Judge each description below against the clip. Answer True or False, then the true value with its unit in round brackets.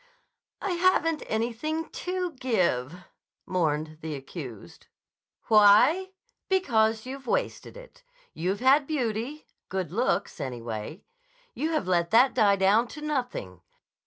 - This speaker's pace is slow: True (115 wpm)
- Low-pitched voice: False (225 Hz)